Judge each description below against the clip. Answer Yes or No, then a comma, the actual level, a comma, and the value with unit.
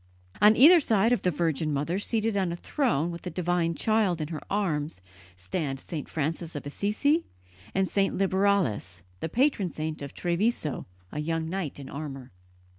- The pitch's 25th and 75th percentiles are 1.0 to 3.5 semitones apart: No, average, 5.0 semitones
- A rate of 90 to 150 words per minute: No, average, 170 wpm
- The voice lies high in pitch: No, medium, 170 Hz